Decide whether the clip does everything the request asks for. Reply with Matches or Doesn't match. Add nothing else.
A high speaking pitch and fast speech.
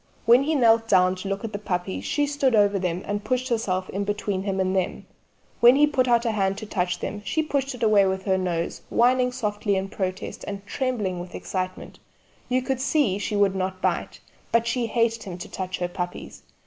Matches